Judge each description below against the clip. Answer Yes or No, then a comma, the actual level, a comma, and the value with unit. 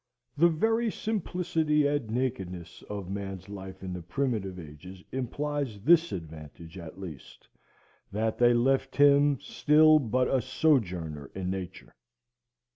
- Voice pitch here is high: No, low, 115 Hz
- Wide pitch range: Yes, wide, 7.8 semitones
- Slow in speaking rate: Yes, slow, 125 wpm